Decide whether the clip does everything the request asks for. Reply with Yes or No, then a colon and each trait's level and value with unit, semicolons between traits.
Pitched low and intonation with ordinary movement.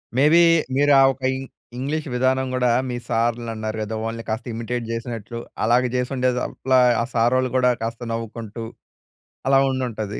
No: low, 120 Hz; narrow, 2.2 semitones